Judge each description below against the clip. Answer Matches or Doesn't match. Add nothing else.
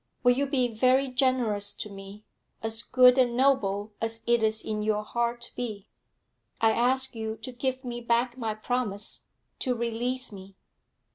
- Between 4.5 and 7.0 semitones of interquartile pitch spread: Doesn't match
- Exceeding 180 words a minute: Doesn't match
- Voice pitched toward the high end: Matches